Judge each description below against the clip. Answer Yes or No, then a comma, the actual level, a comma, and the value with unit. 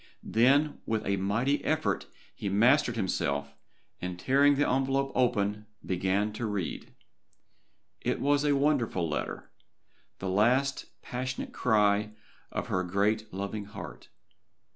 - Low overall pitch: Yes, low, 110 Hz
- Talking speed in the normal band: No, slow, 120 wpm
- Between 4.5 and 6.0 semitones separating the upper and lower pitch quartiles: Yes, average, 5.3 semitones